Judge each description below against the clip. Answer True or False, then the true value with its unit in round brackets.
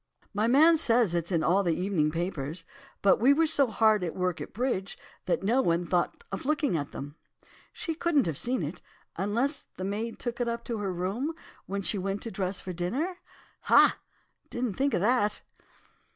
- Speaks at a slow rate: False (195 wpm)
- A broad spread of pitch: True (5.7 semitones)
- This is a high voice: True (205 Hz)